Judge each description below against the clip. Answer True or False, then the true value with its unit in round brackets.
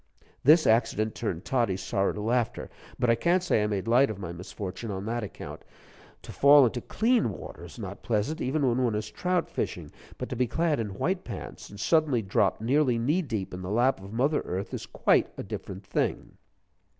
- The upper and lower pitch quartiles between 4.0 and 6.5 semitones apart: True (5.6 semitones)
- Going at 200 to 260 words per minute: True (205 wpm)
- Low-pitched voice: True (115 Hz)